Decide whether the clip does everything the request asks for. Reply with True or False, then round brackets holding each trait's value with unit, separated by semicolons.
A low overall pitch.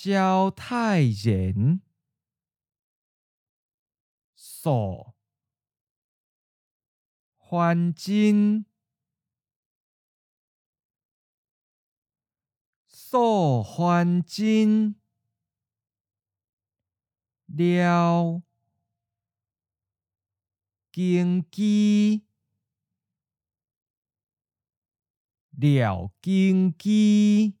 False (155 Hz)